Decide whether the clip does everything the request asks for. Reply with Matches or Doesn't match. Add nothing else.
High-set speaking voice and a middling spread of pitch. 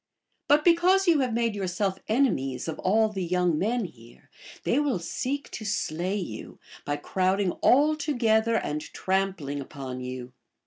Doesn't match